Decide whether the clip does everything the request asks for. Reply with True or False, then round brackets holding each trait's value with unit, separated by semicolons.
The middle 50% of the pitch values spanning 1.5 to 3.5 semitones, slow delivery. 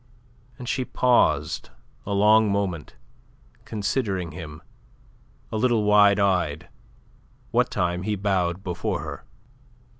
True (3.2 semitones; 110 wpm)